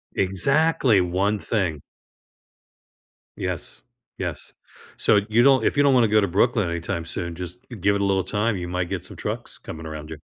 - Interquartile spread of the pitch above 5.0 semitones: No, average, 4.4 semitones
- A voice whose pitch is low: Yes, low, 100 Hz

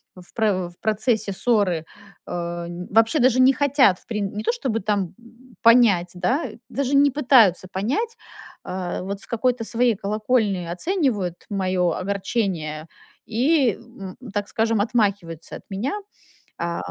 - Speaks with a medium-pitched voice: No, high, 210 Hz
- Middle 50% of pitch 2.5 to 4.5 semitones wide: No, average, 4.9 semitones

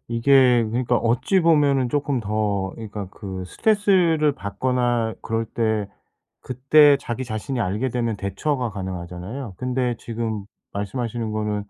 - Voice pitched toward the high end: No, low, 115 Hz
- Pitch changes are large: No, average, 3.8 semitones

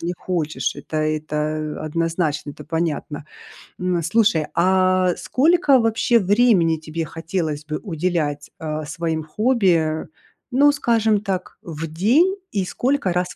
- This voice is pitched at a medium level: Yes, medium, 170 Hz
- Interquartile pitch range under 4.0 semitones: No, average, 5.2 semitones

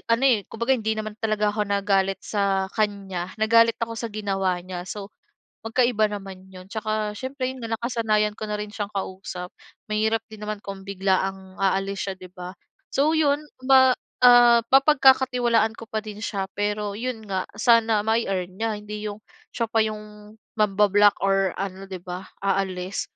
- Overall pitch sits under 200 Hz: No, high, 210 Hz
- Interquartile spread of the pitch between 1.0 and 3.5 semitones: Yes, narrow, 2.6 semitones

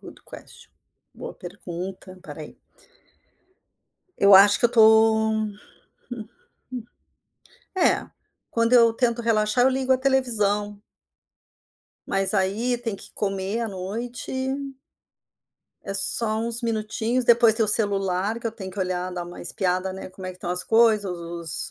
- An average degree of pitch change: Yes, average, 3.5 semitones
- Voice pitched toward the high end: Yes, high, 215 Hz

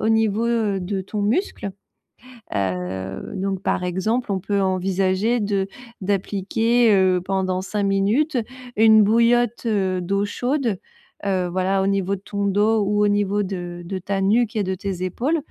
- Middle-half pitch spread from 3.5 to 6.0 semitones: No, average, 2.7 semitones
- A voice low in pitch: No, high, 200 Hz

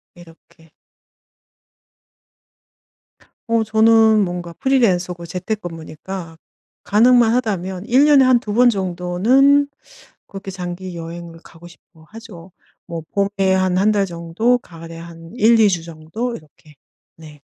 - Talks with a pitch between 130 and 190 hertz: Yes, medium, 185 Hz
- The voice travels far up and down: No, average, 4.8 semitones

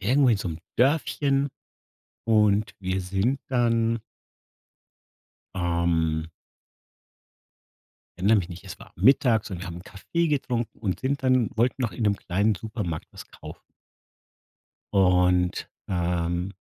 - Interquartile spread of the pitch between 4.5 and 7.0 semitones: Yes, average, 5.2 semitones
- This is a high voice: No, low, 100 Hz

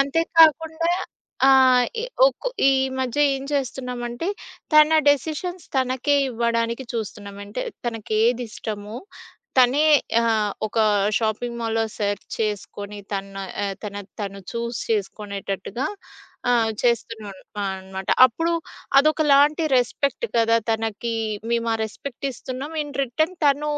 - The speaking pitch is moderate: No, high, 235 Hz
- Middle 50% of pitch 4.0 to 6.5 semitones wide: Yes, average, 4.5 semitones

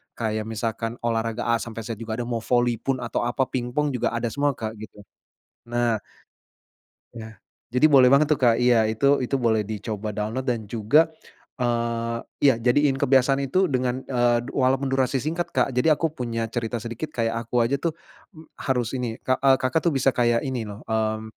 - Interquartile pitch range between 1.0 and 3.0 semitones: Yes, narrow, 2.6 semitones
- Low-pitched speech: Yes, low, 120 Hz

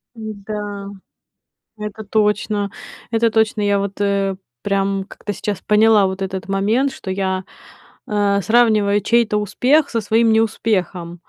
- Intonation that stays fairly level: Yes, narrow, 1.9 semitones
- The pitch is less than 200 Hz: No, high, 205 Hz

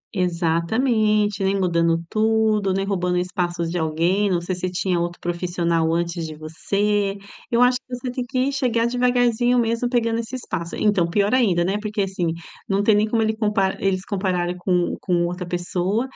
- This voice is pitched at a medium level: No, high, 195 Hz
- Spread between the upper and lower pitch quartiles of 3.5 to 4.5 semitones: Yes, average, 4.2 semitones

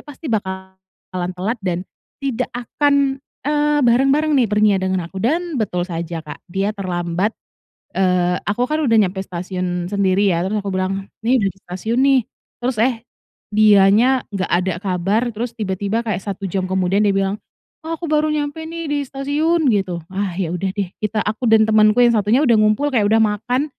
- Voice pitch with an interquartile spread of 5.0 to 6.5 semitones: Yes, average, 5.3 semitones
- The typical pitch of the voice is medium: No, high, 210 Hz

